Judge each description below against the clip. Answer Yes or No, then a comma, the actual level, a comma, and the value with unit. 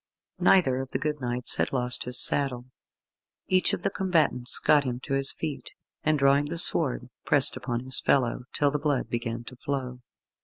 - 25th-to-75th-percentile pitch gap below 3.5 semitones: Yes, average, 2.8 semitones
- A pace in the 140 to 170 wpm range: No, average, 185 wpm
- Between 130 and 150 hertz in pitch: Yes, low, 135 Hz